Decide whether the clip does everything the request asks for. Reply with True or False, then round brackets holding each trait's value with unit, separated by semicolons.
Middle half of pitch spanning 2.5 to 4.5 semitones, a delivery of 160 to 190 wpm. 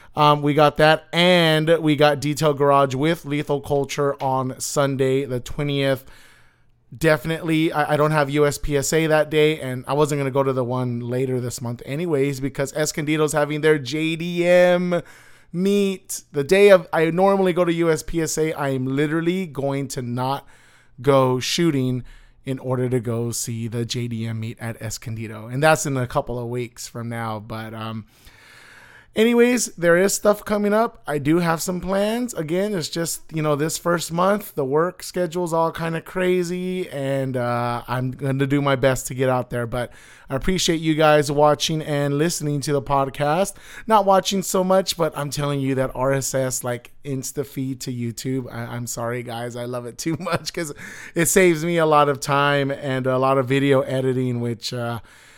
True (4.2 semitones; 185 wpm)